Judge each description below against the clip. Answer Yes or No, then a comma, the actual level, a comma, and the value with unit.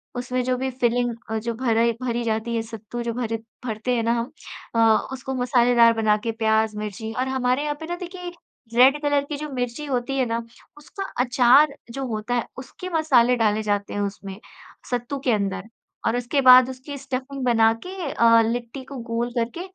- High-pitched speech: Yes, high, 245 Hz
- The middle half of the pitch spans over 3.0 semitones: No, average, 2.7 semitones